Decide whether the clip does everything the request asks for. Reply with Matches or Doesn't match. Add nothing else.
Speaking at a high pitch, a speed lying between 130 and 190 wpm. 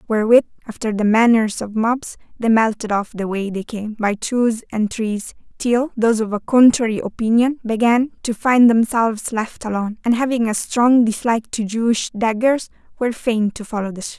Matches